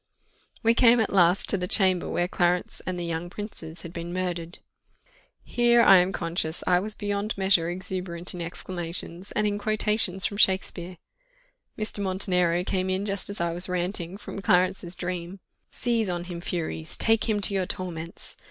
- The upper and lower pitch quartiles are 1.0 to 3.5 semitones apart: Yes, narrow, 2.5 semitones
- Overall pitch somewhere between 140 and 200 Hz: Yes, medium, 185 Hz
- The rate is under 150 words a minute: No, average, 170 wpm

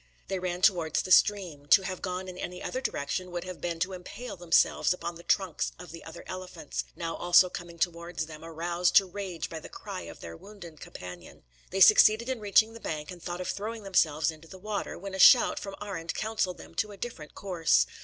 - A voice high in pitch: No, medium, 180 Hz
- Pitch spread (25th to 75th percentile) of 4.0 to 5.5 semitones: No, average, 2.9 semitones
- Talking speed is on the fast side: Yes, fast, 215 wpm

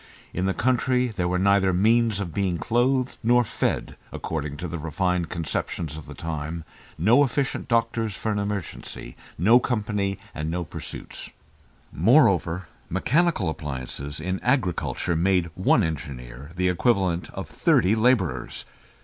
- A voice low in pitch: Yes, very low, 95 Hz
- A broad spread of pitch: Yes, wide, 5.9 semitones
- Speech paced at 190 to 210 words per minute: No, slow, 135 wpm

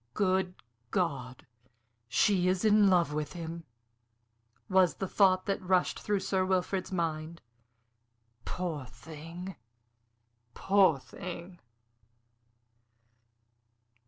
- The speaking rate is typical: No, slow, 90 wpm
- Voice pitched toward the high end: No, medium, 180 Hz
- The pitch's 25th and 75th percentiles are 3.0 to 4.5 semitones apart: No, narrow, 2.6 semitones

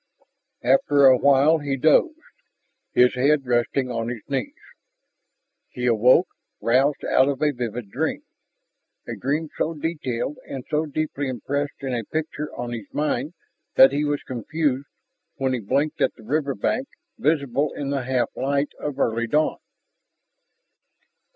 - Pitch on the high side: No, medium, 140 Hz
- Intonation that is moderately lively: Yes, average, 3.2 semitones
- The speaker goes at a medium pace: Yes, average, 145 wpm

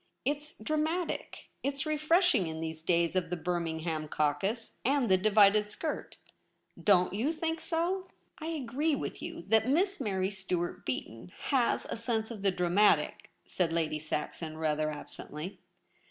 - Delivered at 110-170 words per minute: Yes, average, 155 wpm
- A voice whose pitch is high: Yes, high, 205 Hz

